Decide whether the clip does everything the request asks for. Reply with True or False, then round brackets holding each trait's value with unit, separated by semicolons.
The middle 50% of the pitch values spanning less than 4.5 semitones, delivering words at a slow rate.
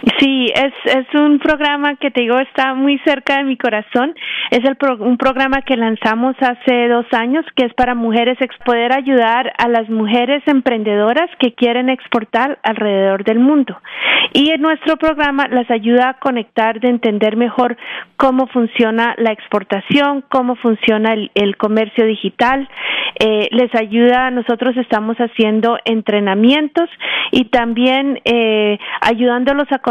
False (3.0 semitones; 150 wpm)